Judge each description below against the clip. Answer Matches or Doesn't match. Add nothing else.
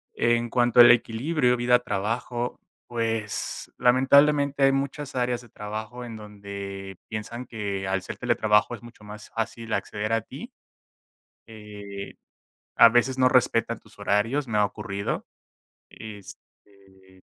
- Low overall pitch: Matches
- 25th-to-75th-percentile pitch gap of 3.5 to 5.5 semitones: Doesn't match